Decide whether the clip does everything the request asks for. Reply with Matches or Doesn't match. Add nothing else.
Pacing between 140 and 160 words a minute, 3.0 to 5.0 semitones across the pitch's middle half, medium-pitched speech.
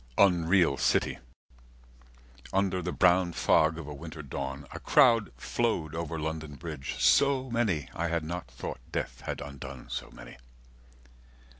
Doesn't match